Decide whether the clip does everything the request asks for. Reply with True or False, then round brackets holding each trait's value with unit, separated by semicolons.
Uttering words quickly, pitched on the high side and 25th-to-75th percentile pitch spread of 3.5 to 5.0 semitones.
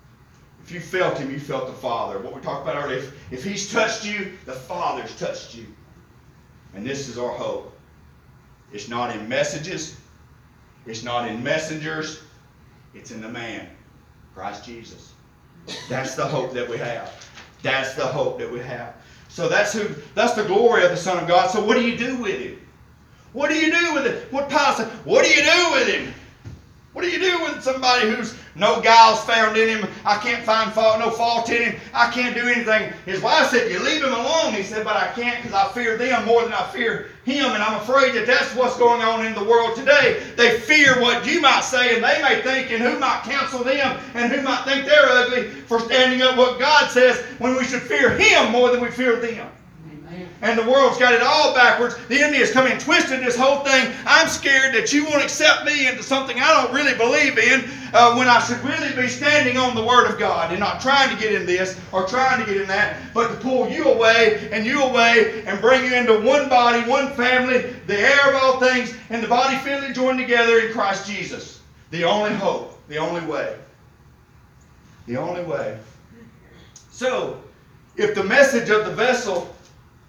True (210 wpm; 240 Hz; 4.1 semitones)